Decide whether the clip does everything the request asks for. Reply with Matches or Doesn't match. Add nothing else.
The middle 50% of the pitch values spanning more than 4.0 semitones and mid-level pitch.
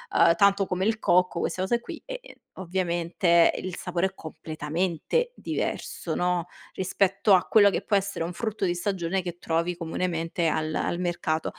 Doesn't match